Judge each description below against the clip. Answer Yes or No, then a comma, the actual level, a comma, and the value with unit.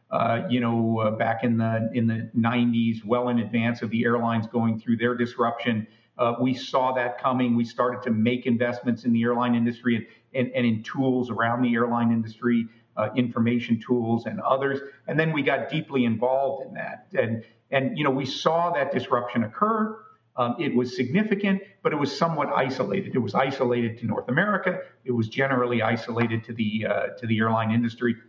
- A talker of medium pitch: No, low, 120 Hz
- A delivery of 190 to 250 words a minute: Yes, average, 195 wpm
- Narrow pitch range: Yes, narrow, 2.0 semitones